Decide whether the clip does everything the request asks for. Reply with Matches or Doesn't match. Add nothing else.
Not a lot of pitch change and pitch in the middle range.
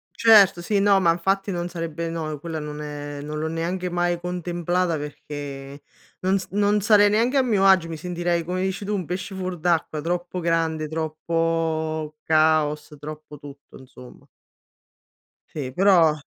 Doesn't match